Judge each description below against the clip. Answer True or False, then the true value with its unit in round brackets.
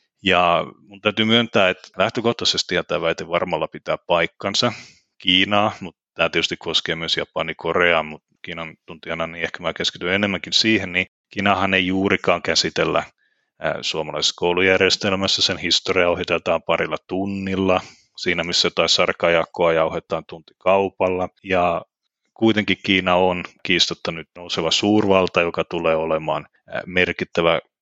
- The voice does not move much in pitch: True (2.1 semitones)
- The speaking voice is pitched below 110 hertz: True (95 Hz)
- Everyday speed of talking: True (125 wpm)